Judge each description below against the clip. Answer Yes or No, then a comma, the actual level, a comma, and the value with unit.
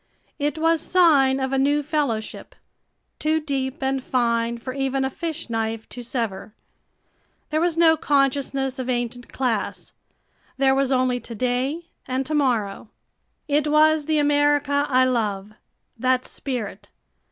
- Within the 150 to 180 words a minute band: No, average, 140 wpm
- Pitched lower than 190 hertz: No, very high, 265 Hz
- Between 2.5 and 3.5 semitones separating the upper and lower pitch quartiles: Yes, average, 3.2 semitones